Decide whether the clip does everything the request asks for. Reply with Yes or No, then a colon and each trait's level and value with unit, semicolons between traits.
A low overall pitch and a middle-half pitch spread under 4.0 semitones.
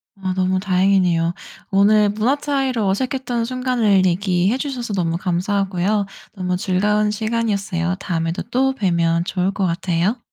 No: high, 195 Hz; average, 3.6 semitones